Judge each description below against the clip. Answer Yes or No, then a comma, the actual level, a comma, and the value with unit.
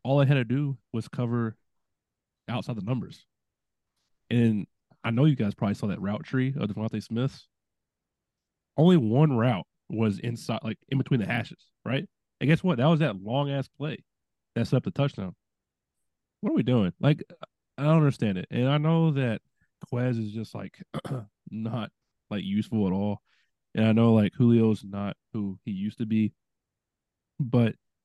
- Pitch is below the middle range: Yes, low, 115 Hz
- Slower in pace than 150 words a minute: No, average, 175 wpm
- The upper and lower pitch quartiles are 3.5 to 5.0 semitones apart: Yes, average, 4.4 semitones